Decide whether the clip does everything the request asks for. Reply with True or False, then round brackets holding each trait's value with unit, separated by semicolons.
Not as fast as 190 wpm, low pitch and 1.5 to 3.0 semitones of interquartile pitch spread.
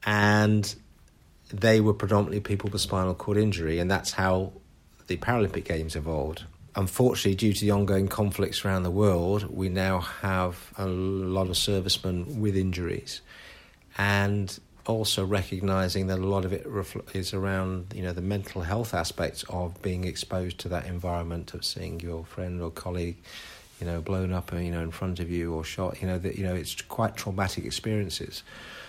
True (170 wpm; 95 Hz; 2.4 semitones)